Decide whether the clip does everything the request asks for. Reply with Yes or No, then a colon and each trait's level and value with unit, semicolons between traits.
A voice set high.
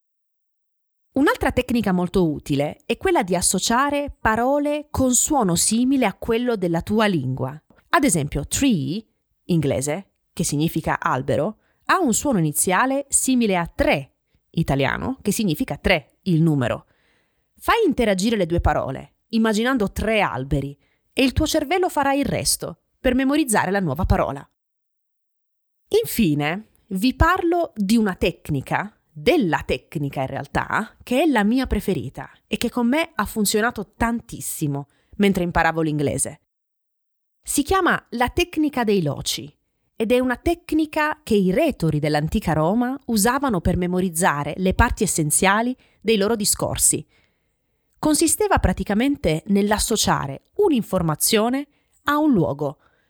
Yes: high, 210 Hz